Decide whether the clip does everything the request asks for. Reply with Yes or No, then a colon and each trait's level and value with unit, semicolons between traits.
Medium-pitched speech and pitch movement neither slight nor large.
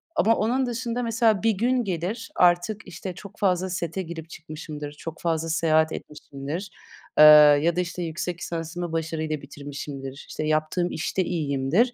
Yes: medium, 170 Hz; average, 3.8 semitones